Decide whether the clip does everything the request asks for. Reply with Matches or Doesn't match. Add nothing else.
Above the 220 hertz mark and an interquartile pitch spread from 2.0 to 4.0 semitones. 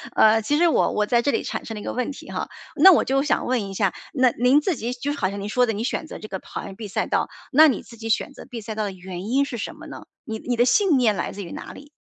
Doesn't match